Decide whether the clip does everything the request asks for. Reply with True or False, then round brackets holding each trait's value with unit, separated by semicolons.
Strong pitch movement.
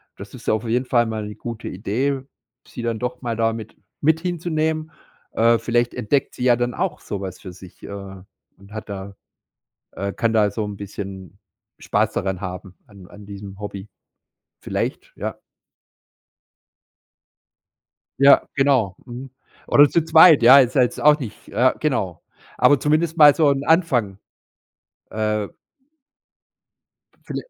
True (5.8 semitones)